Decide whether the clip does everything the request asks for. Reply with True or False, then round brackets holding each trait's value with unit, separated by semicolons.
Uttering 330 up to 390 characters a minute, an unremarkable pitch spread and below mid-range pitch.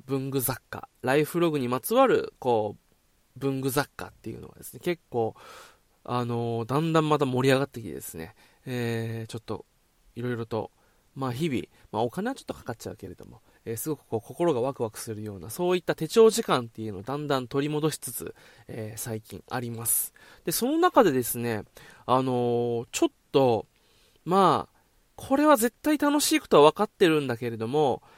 False (370 characters per minute; 5.7 semitones; 130 Hz)